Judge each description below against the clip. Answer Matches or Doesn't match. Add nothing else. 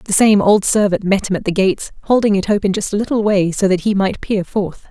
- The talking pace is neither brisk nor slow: Doesn't match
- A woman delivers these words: Matches